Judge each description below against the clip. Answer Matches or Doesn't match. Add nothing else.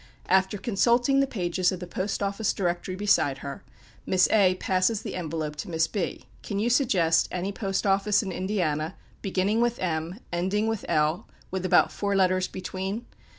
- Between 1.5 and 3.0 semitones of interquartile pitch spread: Matches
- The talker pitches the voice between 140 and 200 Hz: Matches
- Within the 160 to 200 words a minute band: Matches